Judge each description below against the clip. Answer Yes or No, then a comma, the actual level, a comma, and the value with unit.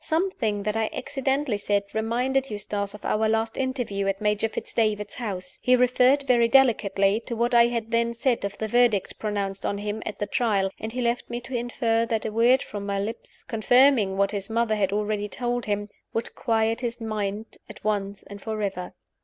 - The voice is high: Yes, high, 220 Hz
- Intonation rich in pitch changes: No, average, 2.8 semitones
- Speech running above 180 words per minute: Yes, average, 195 wpm